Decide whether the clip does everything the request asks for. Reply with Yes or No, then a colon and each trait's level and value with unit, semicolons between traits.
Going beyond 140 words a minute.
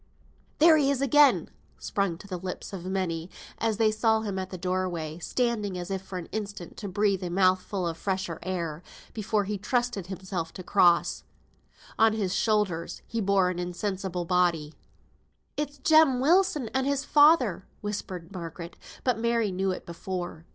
Yes: average, 170 wpm